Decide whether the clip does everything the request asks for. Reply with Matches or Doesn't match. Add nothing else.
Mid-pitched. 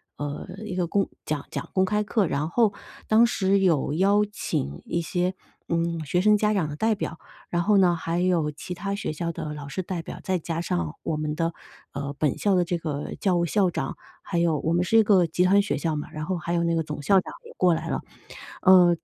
Matches